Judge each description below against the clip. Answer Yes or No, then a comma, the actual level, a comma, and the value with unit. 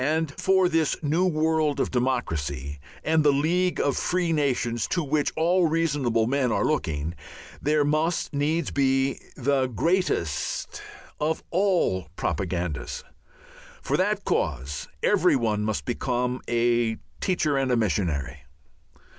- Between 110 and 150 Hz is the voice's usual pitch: Yes, medium, 140 Hz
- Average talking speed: No, slow, 130 wpm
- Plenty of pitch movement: Yes, wide, 6.2 semitones